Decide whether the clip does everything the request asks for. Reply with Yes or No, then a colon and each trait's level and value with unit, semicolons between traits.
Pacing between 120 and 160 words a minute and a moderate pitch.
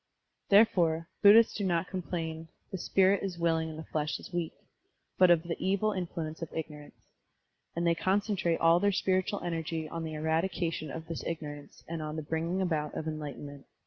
No: average, 185 wpm; medium, 165 Hz